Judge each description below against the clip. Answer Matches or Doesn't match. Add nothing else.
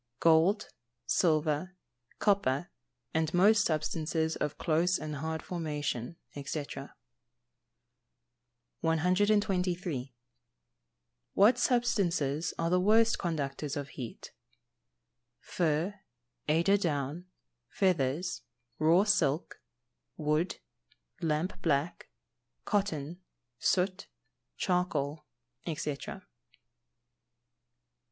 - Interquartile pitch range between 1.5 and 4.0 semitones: Matches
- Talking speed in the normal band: Doesn't match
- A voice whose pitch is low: Doesn't match